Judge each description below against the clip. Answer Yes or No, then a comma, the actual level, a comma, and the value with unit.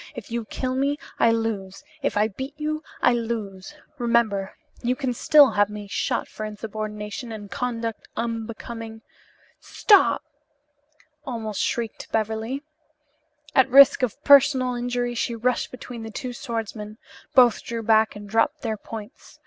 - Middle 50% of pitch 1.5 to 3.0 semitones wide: Yes, narrow, 2.6 semitones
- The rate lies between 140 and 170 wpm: Yes, average, 145 wpm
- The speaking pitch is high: Yes, high, 230 Hz